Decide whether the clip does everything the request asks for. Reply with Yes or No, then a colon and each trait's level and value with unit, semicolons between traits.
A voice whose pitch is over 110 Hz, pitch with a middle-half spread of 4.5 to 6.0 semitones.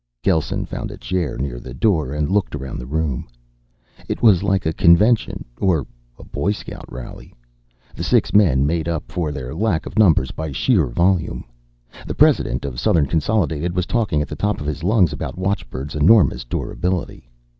No: very low, 80 Hz; average, 4.9 semitones